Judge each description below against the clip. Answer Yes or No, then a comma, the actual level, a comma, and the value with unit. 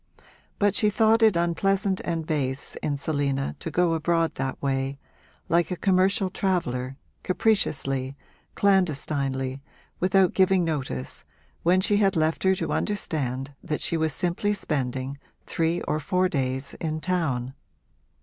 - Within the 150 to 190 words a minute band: No, slow, 135 wpm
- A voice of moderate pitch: Yes, medium, 165 Hz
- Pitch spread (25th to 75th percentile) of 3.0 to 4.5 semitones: No, wide, 5.5 semitones